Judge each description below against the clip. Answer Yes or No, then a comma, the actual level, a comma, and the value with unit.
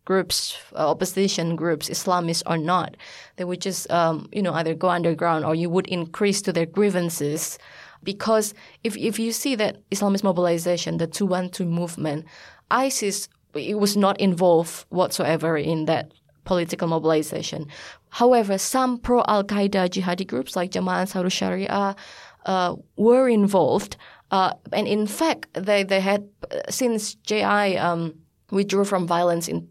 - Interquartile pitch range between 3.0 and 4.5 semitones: Yes, average, 3.3 semitones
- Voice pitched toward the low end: No, medium, 185 Hz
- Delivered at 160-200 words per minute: No, average, 150 wpm